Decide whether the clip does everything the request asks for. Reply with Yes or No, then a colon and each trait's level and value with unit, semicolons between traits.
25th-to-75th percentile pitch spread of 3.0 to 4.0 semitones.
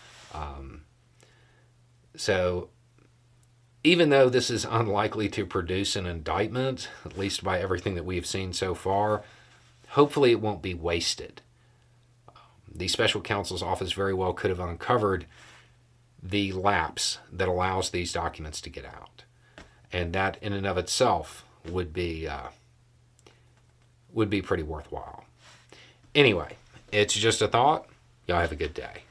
No: average, 4.8 semitones